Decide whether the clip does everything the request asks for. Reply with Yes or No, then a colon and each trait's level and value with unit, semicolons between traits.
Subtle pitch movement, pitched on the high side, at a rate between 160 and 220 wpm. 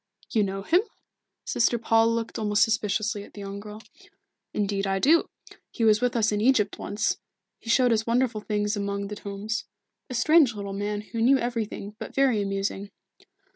Yes: narrow, 2.2 semitones; high, 215 Hz; average, 175 wpm